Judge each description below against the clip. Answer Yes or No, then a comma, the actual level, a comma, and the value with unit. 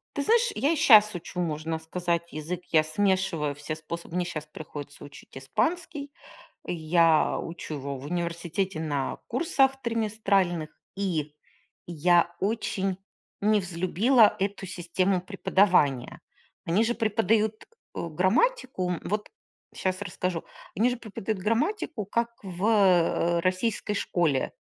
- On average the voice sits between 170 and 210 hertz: Yes, medium, 185 Hz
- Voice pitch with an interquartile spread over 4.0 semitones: Yes, average, 4.7 semitones